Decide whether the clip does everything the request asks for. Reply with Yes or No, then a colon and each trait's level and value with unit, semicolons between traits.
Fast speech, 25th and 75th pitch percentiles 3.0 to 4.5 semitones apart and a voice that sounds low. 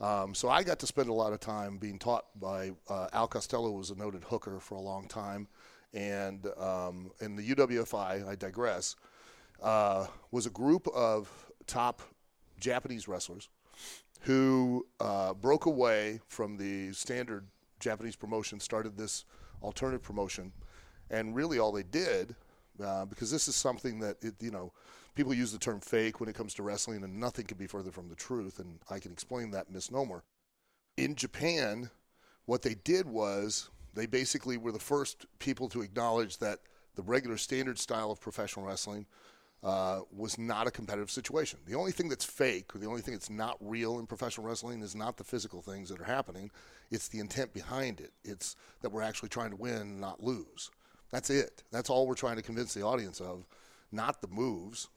No: average, 185 wpm; average, 3.6 semitones; low, 110 Hz